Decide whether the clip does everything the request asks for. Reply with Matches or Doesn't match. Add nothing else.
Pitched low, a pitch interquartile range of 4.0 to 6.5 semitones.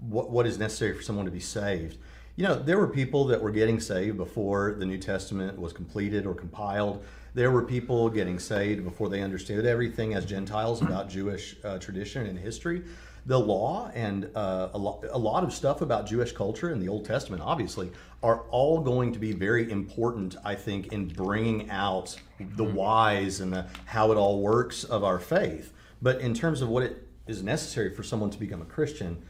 Doesn't match